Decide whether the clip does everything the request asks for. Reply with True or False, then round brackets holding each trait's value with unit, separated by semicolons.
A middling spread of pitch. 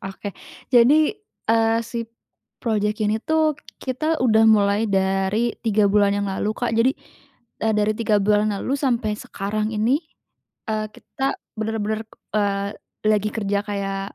False (2.1 semitones)